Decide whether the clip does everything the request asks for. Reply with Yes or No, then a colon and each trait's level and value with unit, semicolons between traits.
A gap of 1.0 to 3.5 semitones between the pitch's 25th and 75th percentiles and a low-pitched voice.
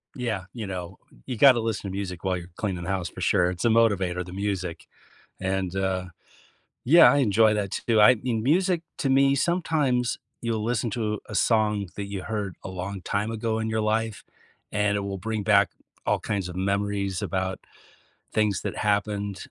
Yes: average, 3.0 semitones; low, 105 Hz